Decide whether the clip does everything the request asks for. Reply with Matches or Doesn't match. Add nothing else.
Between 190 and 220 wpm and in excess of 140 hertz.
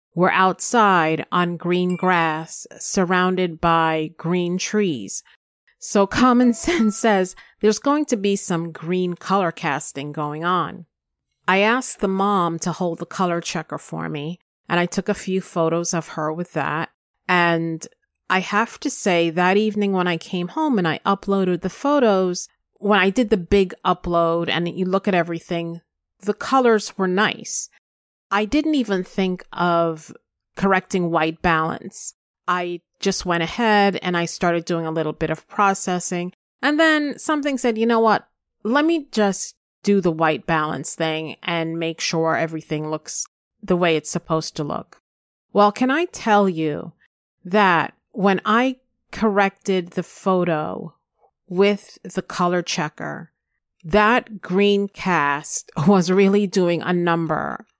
Doesn't match